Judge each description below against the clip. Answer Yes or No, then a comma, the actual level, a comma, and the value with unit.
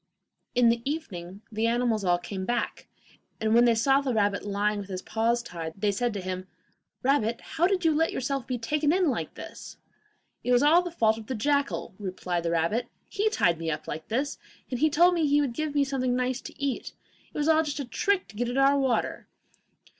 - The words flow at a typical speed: No, fast, 220 wpm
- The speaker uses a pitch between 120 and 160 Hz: No, high, 245 Hz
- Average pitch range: No, wide, 5.7 semitones